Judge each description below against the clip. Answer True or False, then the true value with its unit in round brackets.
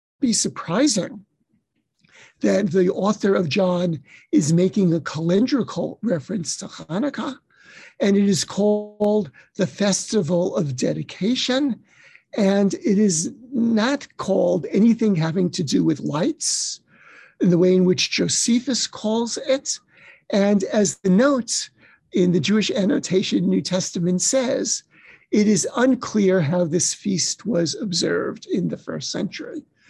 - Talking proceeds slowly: True (125 wpm)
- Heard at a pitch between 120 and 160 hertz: False (200 Hz)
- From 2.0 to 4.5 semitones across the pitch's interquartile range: True (4.0 semitones)